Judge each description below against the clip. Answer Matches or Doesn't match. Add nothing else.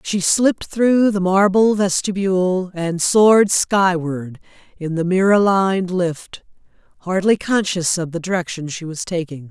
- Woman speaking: Matches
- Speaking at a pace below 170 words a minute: Matches